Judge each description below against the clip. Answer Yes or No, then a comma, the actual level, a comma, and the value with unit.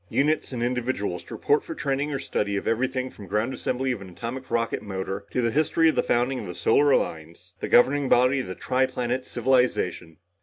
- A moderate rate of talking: No, fast, 215 wpm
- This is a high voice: No, low, 125 Hz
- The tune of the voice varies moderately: Yes, average, 4.4 semitones